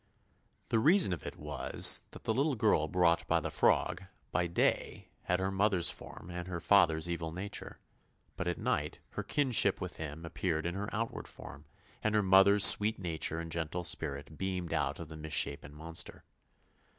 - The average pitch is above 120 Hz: No, very low, 90 Hz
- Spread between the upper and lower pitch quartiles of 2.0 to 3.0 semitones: No, average, 3.7 semitones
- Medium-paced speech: Yes, average, 175 wpm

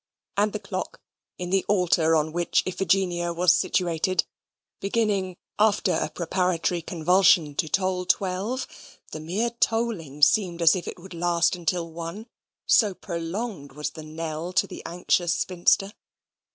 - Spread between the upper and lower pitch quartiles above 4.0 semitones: No, average, 2.7 semitones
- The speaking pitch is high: No, medium, 180 Hz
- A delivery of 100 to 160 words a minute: Yes, average, 140 wpm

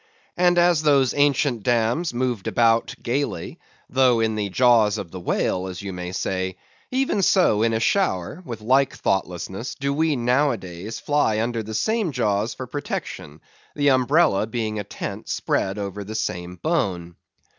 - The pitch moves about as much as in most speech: No, wide, 6.0 semitones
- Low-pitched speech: Yes, low, 115 Hz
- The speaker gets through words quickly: No, average, 165 wpm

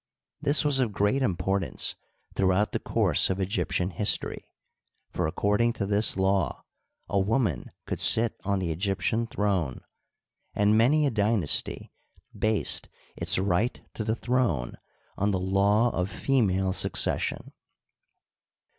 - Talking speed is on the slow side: Yes, slow, 130 wpm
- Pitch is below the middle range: Yes, low, 100 Hz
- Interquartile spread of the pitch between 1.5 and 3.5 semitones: Yes, average, 3.2 semitones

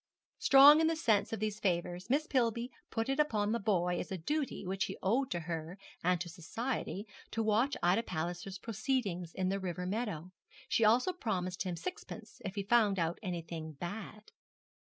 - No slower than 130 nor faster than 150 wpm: No, average, 180 wpm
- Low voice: No, high, 200 Hz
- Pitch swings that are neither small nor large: Yes, average, 4.8 semitones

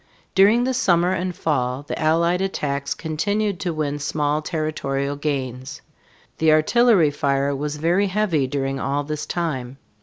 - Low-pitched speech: No, medium, 155 Hz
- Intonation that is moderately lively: Yes, average, 4.2 semitones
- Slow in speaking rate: No, average, 145 wpm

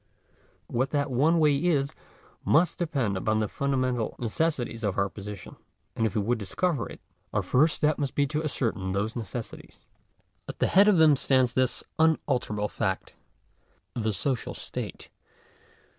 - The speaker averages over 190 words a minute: No, average, 160 wpm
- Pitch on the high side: No, low, 130 Hz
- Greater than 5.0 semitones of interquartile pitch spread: Yes, wide, 5.5 semitones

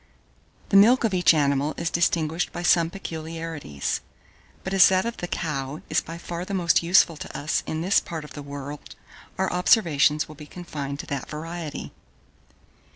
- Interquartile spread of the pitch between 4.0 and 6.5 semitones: No, average, 3.1 semitones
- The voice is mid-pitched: Yes, medium, 165 Hz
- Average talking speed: Yes, average, 175 wpm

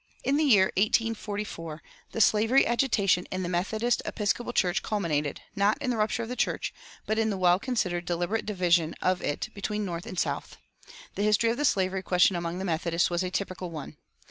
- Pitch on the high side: Yes, high, 195 Hz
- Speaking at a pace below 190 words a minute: No, average, 195 wpm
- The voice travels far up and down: No, average, 3.9 semitones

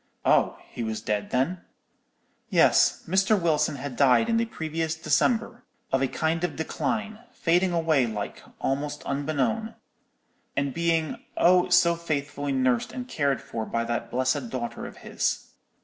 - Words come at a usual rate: Yes, average, 150 wpm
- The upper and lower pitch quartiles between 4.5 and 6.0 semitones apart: Yes, average, 5.1 semitones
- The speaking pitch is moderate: Yes, medium, 155 Hz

